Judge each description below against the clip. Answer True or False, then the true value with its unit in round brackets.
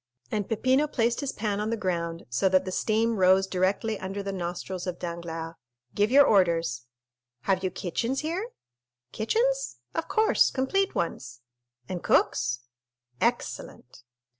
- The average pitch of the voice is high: True (195 Hz)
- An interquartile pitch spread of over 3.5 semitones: True (5.1 semitones)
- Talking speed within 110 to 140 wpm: True (135 wpm)